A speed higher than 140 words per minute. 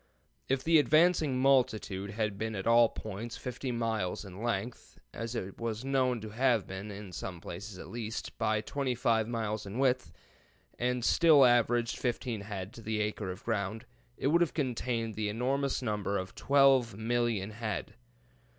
Yes: average, 165 wpm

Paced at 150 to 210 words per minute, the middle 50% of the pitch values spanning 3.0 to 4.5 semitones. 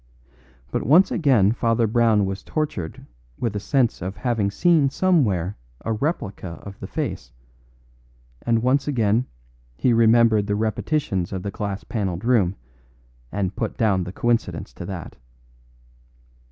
No: average, 140 wpm; average, 3.9 semitones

